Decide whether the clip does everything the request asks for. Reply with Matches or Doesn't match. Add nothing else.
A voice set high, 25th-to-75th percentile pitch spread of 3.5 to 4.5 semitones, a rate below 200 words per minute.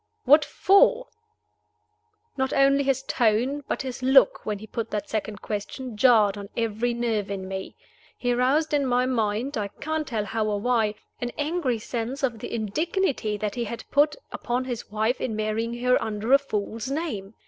Matches